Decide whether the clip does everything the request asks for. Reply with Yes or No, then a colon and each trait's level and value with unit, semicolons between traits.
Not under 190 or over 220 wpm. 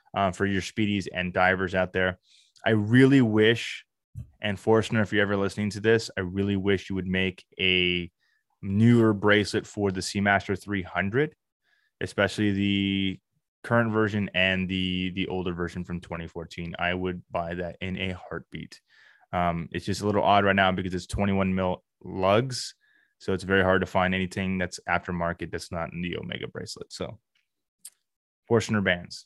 No: average, 165 wpm